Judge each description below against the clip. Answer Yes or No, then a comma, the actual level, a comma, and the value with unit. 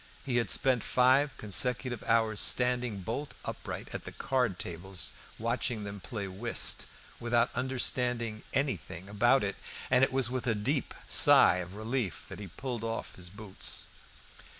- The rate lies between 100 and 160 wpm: Yes, average, 150 wpm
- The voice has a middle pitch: No, low, 115 Hz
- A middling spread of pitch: Yes, average, 3.8 semitones